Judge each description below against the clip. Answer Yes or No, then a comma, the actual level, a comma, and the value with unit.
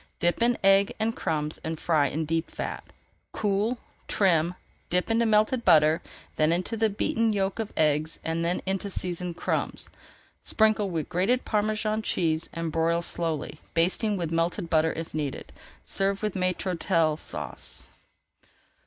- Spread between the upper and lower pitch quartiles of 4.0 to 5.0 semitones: Yes, average, 4.3 semitones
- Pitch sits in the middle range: Yes, medium, 180 Hz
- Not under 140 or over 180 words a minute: Yes, average, 145 wpm